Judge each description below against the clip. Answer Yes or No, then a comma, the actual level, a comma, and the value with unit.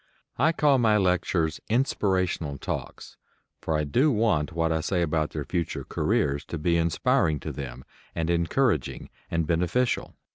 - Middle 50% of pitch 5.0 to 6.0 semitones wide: Yes, average, 5.3 semitones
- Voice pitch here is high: No, very low, 85 Hz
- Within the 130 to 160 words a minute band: Yes, average, 150 wpm